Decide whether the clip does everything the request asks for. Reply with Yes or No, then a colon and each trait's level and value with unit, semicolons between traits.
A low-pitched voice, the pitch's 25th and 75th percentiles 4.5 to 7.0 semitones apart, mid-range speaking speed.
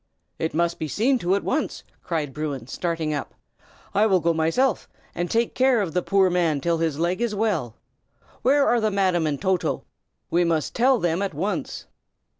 No: medium, 175 Hz; average, 4.8 semitones; average, 190 wpm